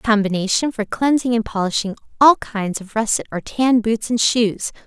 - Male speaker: No, female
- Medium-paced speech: Yes, average, 175 wpm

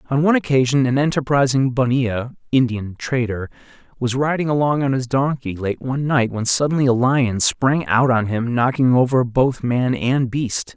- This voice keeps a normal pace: Yes, average, 175 wpm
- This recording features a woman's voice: No, male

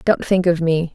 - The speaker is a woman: Yes, female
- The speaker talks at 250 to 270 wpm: Yes, fast, 255 wpm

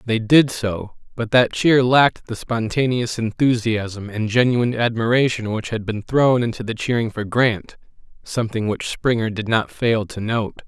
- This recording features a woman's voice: No, male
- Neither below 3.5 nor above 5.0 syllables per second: Yes, 4.5 syllables/s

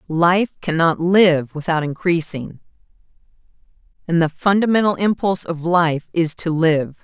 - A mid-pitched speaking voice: Yes, medium, 170 Hz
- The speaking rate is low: Yes, slow, 120 wpm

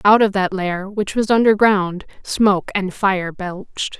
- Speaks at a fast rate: No, average, 165 wpm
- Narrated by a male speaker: No, female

